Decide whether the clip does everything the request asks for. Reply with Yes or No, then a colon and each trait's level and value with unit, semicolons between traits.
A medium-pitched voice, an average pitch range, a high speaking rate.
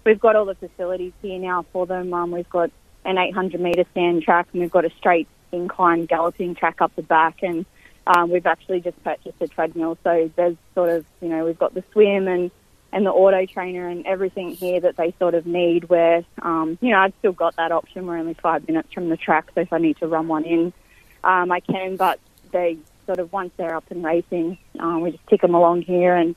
No: medium, 175 Hz; narrow, 1.6 semitones; fast, 235 wpm